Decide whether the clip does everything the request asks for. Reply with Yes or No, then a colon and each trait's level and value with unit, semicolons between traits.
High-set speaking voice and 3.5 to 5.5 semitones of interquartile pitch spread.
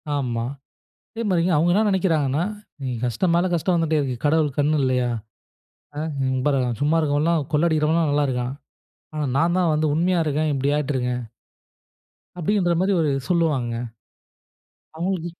No: medium, 155 Hz; average, 3.8 semitones